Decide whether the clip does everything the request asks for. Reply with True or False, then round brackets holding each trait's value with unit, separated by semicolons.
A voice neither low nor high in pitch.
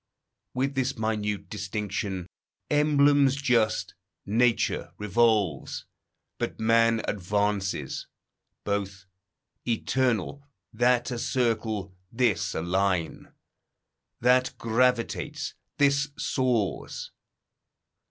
False (115 Hz)